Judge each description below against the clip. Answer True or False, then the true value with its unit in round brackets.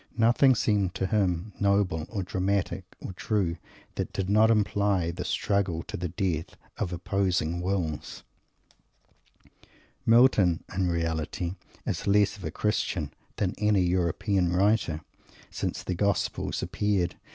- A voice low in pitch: True (95 Hz)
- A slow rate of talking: True (130 wpm)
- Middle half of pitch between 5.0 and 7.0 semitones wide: False (2.8 semitones)